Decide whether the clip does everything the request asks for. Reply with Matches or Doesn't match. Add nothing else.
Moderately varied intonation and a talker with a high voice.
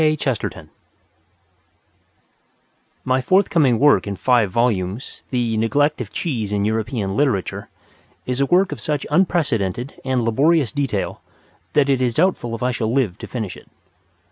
Doesn't match